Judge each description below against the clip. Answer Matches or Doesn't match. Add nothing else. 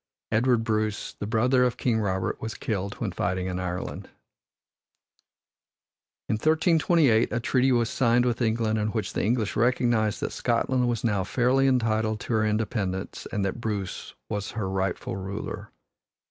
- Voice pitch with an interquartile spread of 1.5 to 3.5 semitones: Matches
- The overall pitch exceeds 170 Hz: Doesn't match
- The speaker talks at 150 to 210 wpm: Matches